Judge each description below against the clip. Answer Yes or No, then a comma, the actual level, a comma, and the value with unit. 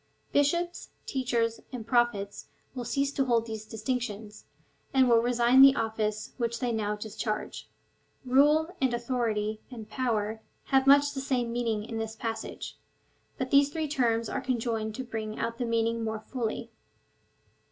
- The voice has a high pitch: Yes, high, 235 Hz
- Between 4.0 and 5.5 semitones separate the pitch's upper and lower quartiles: No, average, 2.9 semitones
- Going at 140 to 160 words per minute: Yes, average, 150 wpm